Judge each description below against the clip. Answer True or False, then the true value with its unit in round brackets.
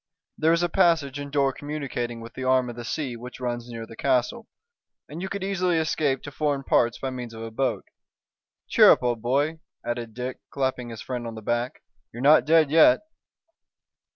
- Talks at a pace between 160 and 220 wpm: True (200 wpm)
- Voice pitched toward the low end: True (130 Hz)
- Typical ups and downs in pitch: True (4.2 semitones)